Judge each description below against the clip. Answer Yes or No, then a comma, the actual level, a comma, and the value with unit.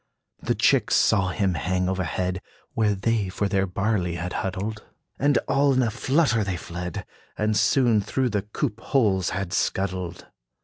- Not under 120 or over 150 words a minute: No, average, 160 wpm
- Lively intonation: No, average, 3.3 semitones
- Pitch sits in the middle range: No, low, 100 Hz